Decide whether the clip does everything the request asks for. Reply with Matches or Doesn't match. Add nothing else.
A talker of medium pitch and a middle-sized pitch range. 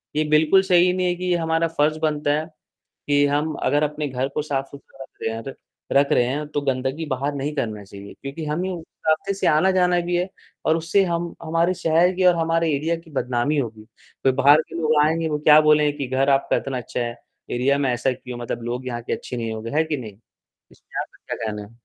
Matches